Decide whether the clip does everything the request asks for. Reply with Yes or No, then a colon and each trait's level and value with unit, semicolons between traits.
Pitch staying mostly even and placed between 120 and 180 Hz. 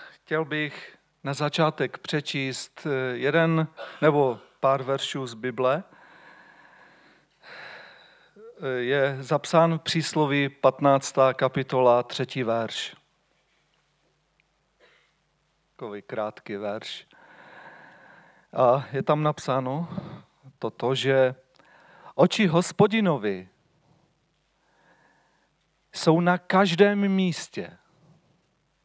No: average, 3.9 semitones; medium, 140 Hz